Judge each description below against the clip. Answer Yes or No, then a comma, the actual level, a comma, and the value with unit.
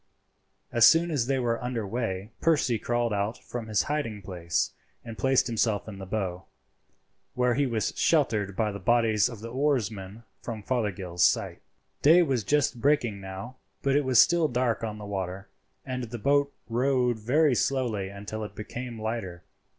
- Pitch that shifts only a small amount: No, average, 3.9 semitones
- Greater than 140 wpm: Yes, average, 170 wpm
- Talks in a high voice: No, low, 115 Hz